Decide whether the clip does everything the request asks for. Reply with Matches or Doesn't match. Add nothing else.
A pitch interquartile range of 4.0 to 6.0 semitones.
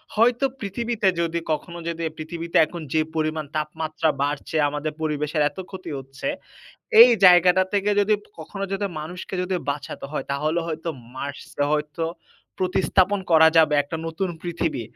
Doesn't match